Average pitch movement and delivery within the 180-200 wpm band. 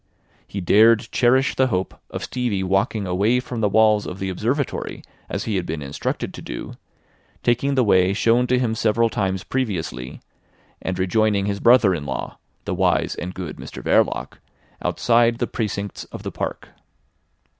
No: average, 4.1 semitones; average, 165 wpm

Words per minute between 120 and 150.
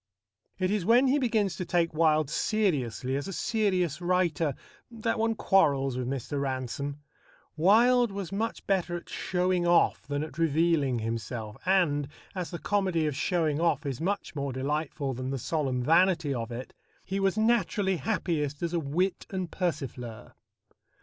No: average, 160 wpm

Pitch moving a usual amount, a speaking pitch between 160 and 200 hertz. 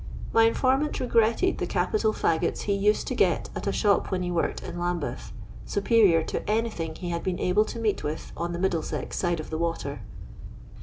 Yes: average, 4.6 semitones; medium, 185 Hz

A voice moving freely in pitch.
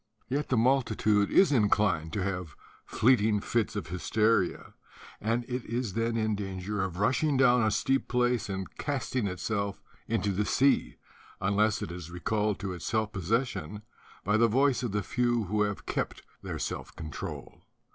No: average, 3.7 semitones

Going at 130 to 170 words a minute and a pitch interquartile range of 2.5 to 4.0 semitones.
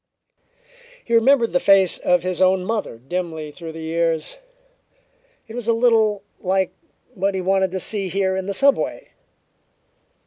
Yes: average, 150 wpm; average, 3.6 semitones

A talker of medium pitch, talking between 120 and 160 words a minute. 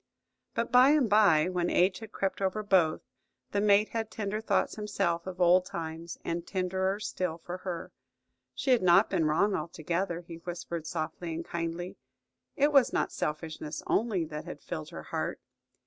No: medium, 180 Hz; average, 170 wpm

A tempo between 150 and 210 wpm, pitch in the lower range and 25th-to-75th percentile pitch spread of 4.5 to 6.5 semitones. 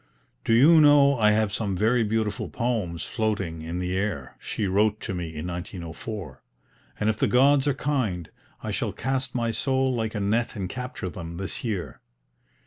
Yes: average, 180 wpm; low, 105 Hz; average, 5.3 semitones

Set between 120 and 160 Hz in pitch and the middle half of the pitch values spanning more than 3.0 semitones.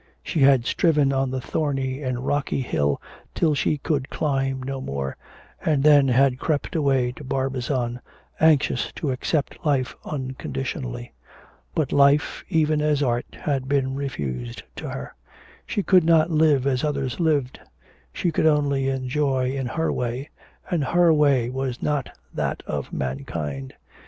No: low, 135 Hz; average, 2.7 semitones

